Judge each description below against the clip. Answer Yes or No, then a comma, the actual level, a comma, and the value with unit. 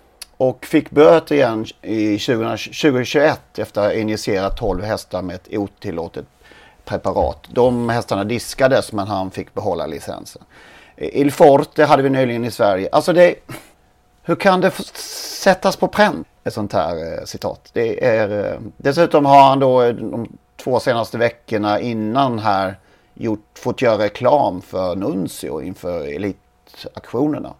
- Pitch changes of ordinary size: No, wide, 6.3 semitones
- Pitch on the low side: Yes, low, 125 Hz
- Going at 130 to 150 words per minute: Yes, average, 140 wpm